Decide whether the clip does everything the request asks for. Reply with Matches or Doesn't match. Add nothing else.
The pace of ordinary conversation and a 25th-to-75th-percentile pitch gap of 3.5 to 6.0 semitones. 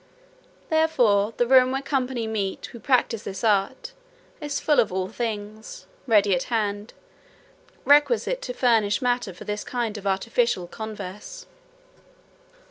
Doesn't match